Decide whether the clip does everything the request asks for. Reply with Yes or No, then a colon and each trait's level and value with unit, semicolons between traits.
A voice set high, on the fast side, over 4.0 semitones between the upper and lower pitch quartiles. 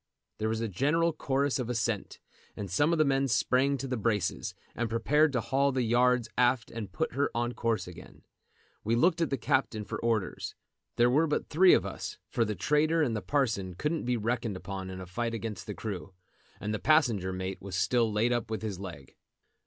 No: low, 115 Hz; fast, 215 wpm; average, 4.8 semitones